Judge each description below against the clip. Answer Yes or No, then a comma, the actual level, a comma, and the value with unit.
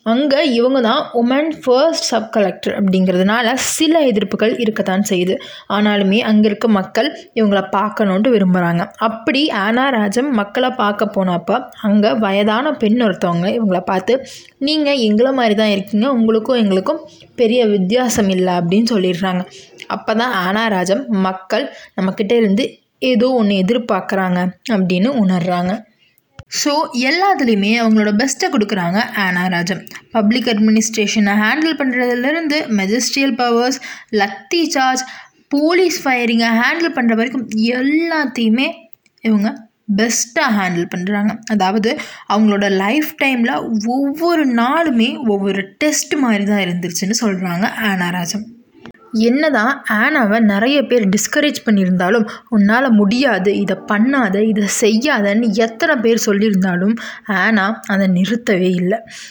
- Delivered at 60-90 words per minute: No, average, 110 wpm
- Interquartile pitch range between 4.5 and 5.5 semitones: No, average, 4.0 semitones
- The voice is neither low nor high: No, high, 225 Hz